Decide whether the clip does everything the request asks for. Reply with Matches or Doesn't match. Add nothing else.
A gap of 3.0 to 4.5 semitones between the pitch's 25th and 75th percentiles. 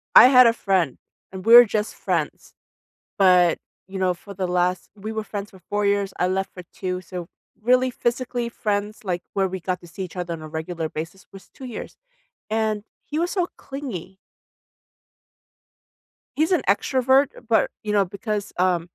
Matches